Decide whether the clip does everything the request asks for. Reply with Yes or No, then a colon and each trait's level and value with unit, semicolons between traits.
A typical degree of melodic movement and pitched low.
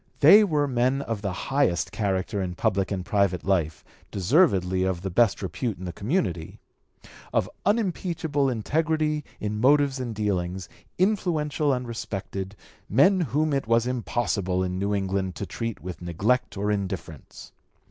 No: wide, 7.0 semitones; low, 105 Hz